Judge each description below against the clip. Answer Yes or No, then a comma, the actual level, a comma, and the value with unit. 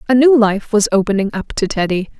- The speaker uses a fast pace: Yes, fast, 220 wpm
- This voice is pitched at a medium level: No, high, 215 Hz